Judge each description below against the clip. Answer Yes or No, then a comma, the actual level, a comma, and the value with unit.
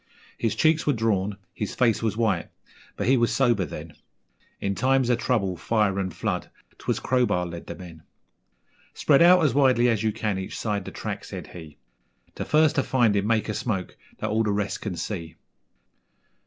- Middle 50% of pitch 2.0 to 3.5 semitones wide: No, average, 4.3 semitones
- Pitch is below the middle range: Yes, low, 110 Hz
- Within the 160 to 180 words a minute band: No, average, 190 wpm